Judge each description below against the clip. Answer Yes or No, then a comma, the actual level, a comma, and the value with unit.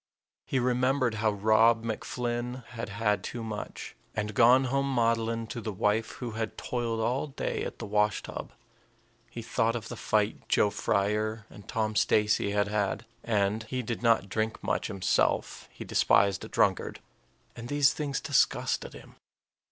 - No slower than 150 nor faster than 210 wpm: Yes, average, 160 wpm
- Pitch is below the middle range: Yes, low, 115 Hz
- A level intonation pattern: Yes, narrow, 2.3 semitones